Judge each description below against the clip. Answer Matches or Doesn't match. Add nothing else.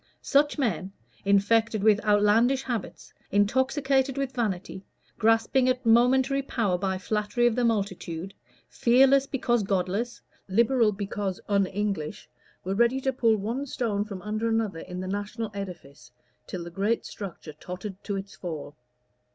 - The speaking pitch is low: Doesn't match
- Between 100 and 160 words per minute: Matches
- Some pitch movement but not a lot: Matches